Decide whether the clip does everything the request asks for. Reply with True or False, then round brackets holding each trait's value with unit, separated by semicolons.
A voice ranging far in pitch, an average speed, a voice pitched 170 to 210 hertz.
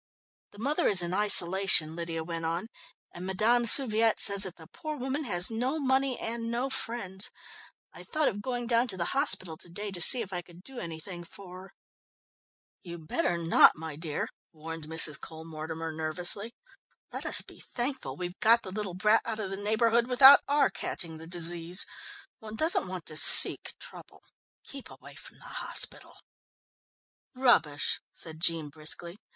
True (5.9 semitones; 170 wpm; 190 Hz)